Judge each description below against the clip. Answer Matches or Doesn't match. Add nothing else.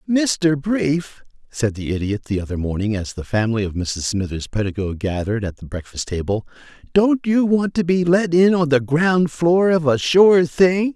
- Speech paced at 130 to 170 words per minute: Doesn't match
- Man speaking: Matches